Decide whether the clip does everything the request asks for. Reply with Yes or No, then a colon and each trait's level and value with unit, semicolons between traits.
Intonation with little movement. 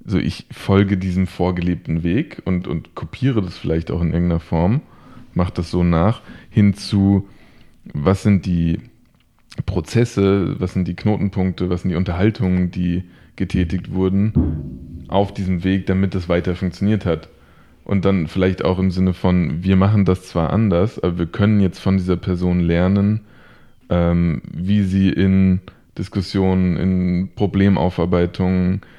Yes: narrow, 2.0 semitones